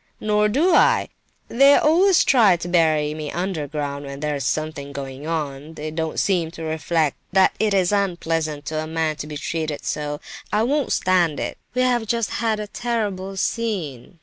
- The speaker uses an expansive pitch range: Yes, wide, 5.7 semitones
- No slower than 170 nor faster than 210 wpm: Yes, average, 175 wpm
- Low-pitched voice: No, medium, 165 Hz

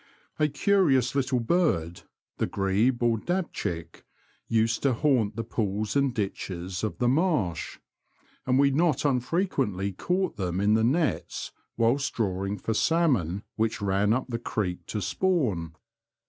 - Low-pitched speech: Yes, low, 115 Hz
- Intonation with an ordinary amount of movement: No, wide, 6.2 semitones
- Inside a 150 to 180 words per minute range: No, average, 140 wpm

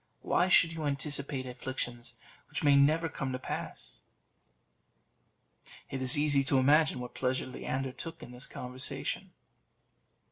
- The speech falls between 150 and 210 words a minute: No, slow, 135 wpm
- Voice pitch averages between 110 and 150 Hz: Yes, low, 135 Hz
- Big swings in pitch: No, narrow, 2.6 semitones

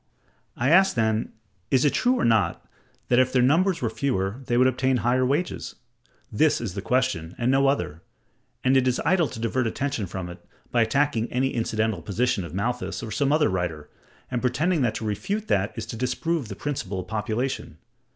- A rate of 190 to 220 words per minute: Yes, average, 195 wpm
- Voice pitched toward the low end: Yes, low, 125 Hz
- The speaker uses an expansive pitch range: No, average, 4.4 semitones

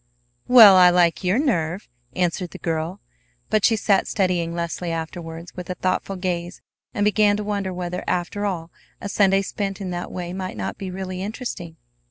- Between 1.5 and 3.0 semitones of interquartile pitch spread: Yes, narrow, 2.5 semitones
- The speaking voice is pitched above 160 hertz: Yes, medium, 185 Hz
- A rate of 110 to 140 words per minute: No, average, 180 wpm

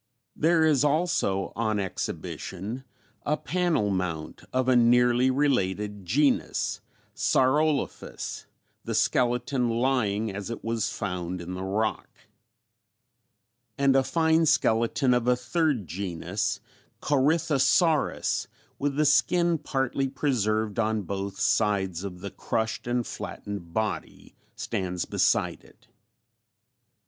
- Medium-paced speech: No, slow, 110 wpm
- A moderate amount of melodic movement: No, wide, 5.9 semitones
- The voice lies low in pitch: Yes, low, 120 Hz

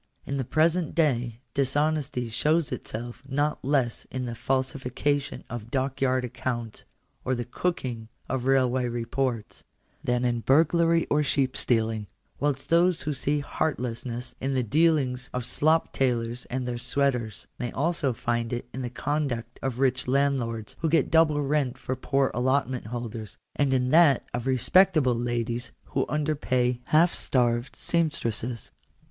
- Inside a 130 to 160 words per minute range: Yes, average, 155 wpm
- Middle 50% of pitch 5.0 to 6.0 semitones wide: No, average, 3.2 semitones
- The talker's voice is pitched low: Yes, low, 130 Hz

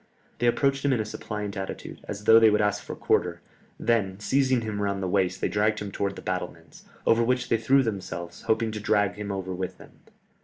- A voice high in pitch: No, low, 105 Hz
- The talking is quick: Yes, fast, 220 wpm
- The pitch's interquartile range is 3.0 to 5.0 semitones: No, narrow, 2.6 semitones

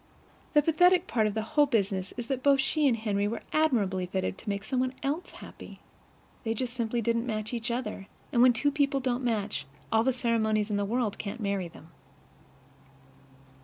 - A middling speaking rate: Yes, average, 195 wpm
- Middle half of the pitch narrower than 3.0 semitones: No, average, 4.0 semitones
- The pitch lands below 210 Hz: No, high, 230 Hz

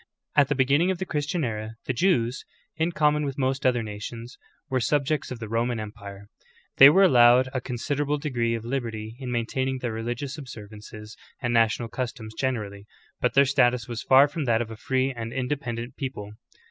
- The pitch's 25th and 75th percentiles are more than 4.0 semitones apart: No, average, 3.3 semitones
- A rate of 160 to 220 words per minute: Yes, average, 185 wpm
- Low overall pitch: Yes, low, 125 Hz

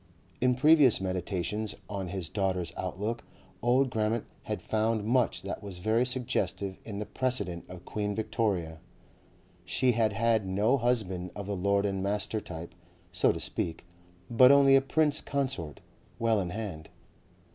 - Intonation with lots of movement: No, average, 4.3 semitones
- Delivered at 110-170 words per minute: Yes, average, 150 wpm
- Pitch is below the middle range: Yes, low, 105 Hz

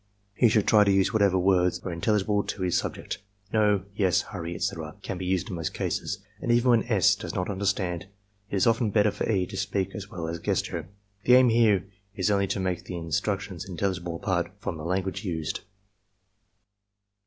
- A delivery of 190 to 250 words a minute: Yes, average, 200 wpm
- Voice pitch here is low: Yes, very low, 95 Hz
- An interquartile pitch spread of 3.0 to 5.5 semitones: No, narrow, 2.6 semitones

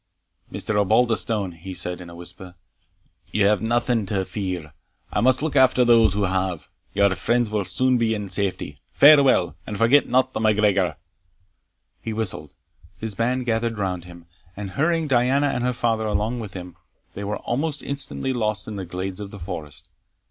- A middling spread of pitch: Yes, average, 4.4 semitones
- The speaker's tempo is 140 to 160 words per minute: No, average, 175 wpm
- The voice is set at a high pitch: No, low, 105 Hz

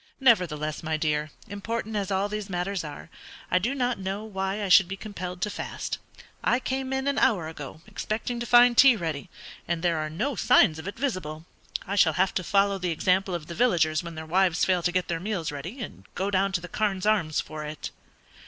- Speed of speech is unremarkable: No, fast, 220 wpm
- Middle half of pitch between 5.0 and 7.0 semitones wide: No, average, 4.5 semitones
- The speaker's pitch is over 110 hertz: Yes, high, 190 Hz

